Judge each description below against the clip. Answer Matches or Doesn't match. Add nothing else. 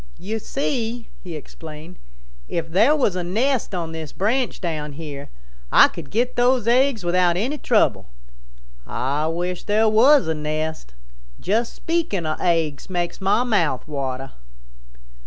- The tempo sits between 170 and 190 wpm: Doesn't match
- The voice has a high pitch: Doesn't match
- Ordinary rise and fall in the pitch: Doesn't match